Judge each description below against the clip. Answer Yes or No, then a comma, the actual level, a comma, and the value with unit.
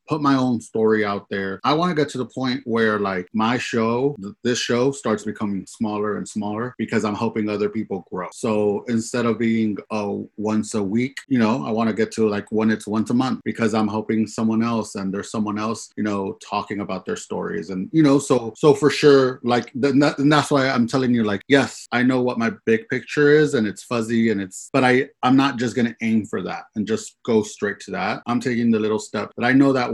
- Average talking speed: No, fast, 245 wpm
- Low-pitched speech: Yes, low, 115 Hz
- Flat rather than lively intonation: No, average, 3.1 semitones